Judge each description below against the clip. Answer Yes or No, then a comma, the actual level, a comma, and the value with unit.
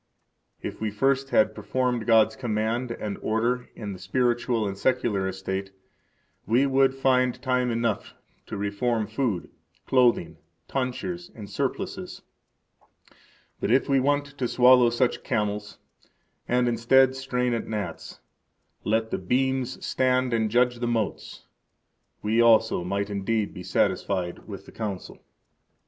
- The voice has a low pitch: Yes, low, 115 Hz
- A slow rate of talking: Yes, slow, 130 wpm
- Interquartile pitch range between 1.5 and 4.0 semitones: Yes, average, 3.3 semitones